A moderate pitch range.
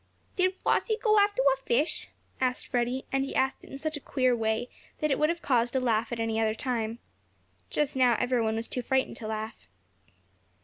Yes: average, 3.2 semitones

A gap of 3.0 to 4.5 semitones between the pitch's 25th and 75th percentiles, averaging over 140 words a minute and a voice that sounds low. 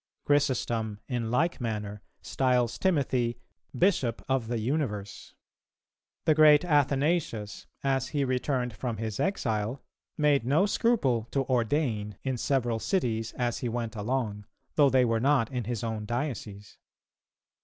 No: average, 4.1 semitones; slow, 135 wpm; low, 125 Hz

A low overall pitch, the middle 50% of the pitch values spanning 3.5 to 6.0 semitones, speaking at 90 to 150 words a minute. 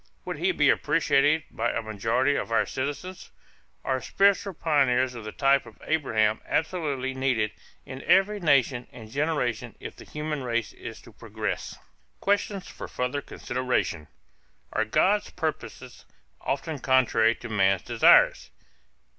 Yes: low, 130 Hz; average, 4.8 semitones; average, 140 wpm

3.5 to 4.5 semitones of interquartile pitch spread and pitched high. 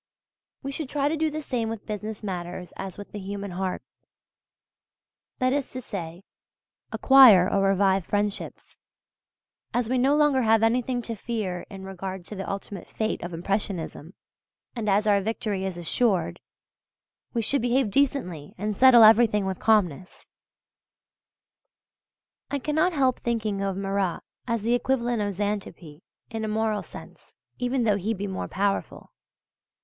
Yes: average, 4.0 semitones; high, 210 Hz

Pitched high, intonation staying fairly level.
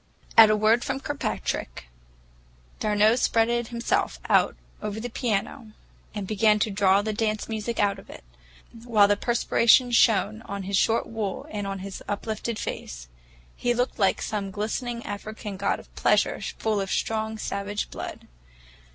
Yes: high, 215 Hz; narrow, 2.3 semitones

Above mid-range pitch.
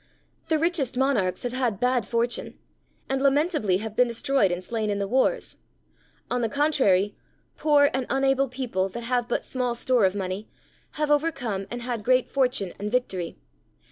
Yes: high, 245 Hz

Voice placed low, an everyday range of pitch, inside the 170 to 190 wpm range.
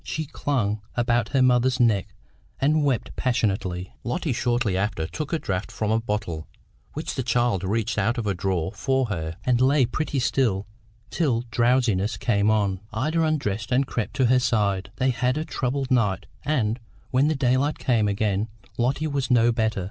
Yes: low, 120 Hz; average, 4.2 semitones; average, 175 wpm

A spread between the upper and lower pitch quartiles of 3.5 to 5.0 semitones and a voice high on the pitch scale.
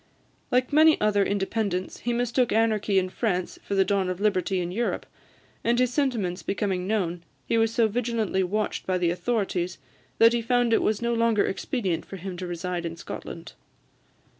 Yes: average, 4.1 semitones; high, 205 Hz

